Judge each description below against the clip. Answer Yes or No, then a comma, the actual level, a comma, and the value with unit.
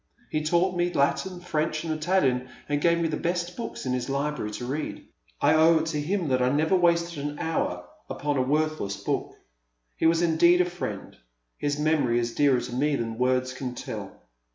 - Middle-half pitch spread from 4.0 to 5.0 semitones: Yes, average, 4.7 semitones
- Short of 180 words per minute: No, average, 200 wpm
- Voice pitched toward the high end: No, medium, 150 Hz